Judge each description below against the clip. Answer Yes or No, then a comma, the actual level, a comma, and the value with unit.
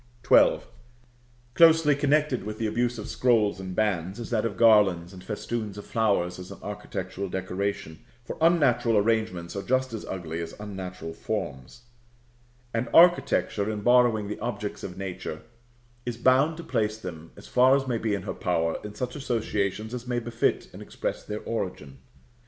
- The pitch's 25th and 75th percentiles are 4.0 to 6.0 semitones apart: Yes, average, 4.4 semitones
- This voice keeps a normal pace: Yes, average, 170 wpm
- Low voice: Yes, low, 110 Hz